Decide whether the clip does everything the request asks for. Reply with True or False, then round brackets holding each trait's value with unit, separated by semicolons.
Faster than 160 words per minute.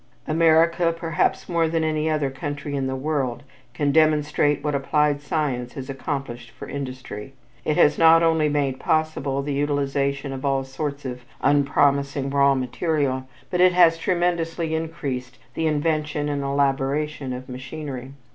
False (145 wpm)